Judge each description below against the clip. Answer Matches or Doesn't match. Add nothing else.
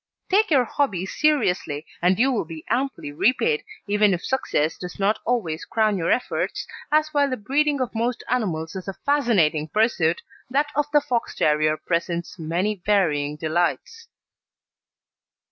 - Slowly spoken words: Doesn't match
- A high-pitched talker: Matches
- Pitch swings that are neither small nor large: Doesn't match